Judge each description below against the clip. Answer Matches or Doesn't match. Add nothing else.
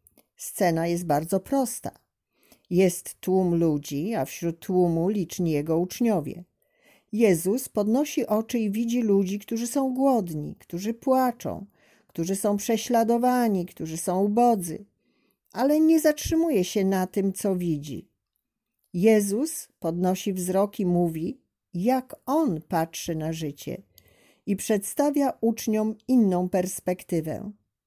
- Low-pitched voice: Doesn't match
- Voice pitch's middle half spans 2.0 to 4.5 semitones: Doesn't match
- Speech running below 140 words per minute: Matches